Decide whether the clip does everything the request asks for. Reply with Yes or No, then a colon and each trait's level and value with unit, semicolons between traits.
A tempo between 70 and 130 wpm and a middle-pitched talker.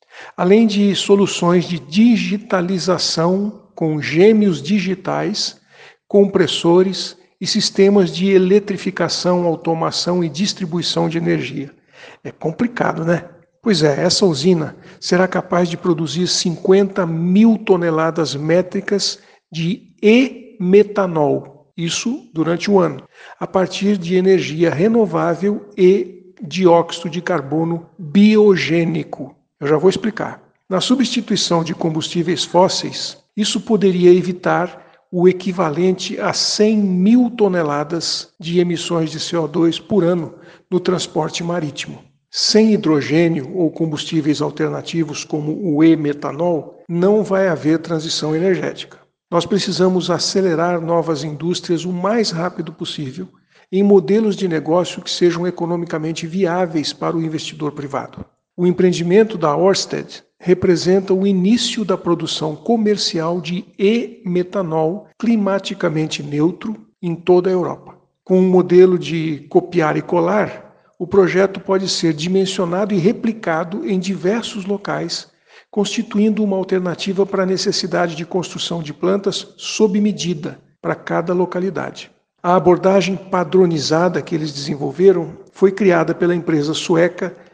Yes: slow, 120 wpm; medium, 180 Hz